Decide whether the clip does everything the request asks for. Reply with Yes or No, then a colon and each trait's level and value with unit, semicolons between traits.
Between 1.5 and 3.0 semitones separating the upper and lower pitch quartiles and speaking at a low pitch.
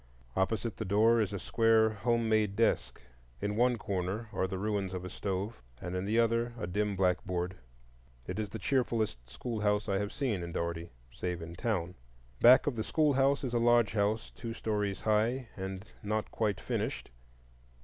No: average, 3.4 semitones; low, 105 Hz